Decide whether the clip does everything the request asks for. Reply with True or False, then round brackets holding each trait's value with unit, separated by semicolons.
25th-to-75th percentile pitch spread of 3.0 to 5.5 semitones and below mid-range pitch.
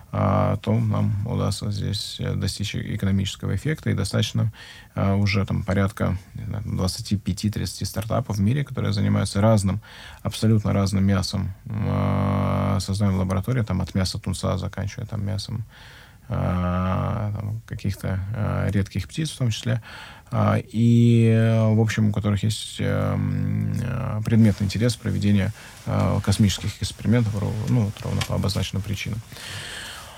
False (2.4 semitones; 105 Hz)